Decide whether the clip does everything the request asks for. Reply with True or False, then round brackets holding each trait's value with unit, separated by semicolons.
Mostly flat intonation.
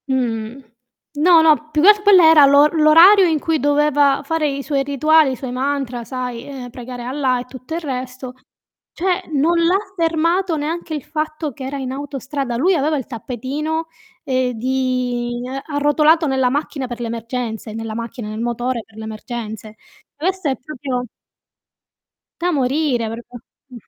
False (3.8 semitones)